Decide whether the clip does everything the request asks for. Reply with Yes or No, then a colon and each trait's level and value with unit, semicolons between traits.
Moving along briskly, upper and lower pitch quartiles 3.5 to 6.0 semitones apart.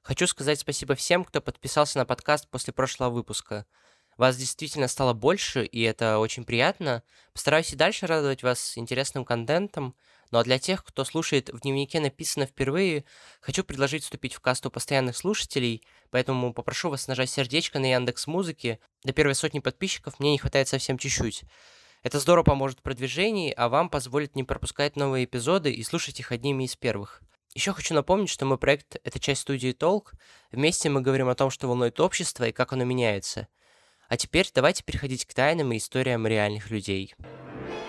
No: fast, 175 wpm; average, 3.0 semitones